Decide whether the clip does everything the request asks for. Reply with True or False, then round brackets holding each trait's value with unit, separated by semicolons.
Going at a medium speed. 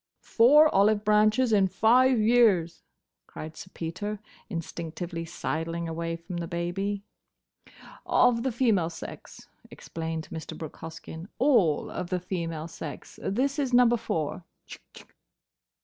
False (120 wpm)